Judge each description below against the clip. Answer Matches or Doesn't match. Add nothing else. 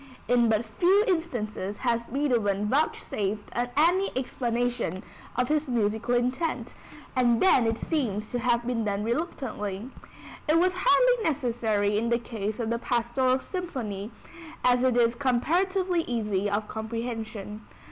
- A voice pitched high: Matches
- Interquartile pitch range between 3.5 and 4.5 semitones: Matches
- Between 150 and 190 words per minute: Doesn't match